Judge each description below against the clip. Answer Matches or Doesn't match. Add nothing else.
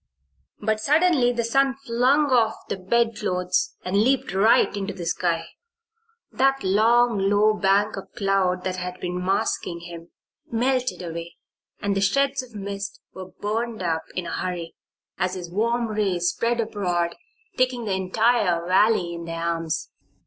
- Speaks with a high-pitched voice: Matches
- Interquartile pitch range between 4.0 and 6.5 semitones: Matches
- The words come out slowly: Doesn't match